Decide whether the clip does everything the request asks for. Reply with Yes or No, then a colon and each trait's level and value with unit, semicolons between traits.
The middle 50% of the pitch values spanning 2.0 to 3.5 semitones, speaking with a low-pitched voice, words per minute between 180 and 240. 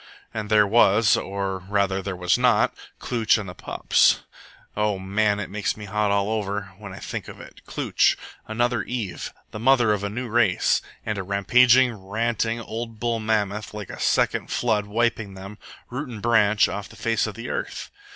Yes: narrow, 2.5 semitones; low, 105 Hz; average, 190 wpm